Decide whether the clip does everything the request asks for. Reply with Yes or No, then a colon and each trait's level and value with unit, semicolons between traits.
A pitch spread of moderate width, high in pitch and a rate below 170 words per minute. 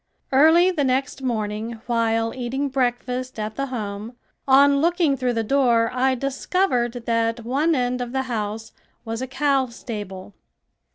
Yes: average, 3.1 semitones; very high, 250 Hz; average, 150 wpm